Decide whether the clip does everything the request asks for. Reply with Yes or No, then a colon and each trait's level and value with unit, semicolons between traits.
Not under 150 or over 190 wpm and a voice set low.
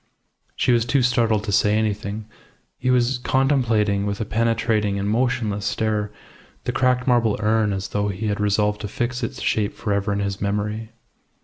Yes: average, 180 wpm; low, 110 Hz